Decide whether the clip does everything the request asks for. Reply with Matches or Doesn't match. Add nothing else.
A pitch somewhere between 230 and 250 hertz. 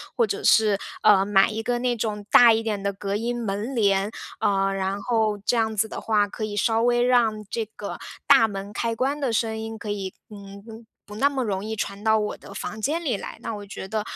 Doesn't match